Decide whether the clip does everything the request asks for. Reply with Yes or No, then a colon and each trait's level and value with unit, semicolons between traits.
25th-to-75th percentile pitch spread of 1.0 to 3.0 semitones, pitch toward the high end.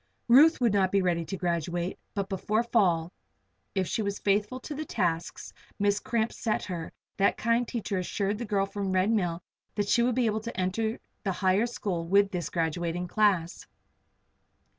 No: average, 3.6 semitones; high, 200 Hz